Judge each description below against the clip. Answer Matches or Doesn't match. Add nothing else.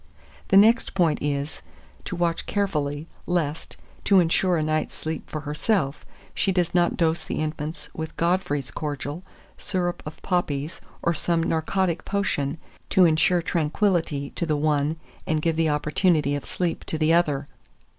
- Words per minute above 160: Doesn't match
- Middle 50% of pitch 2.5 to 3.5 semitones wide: Matches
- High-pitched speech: Doesn't match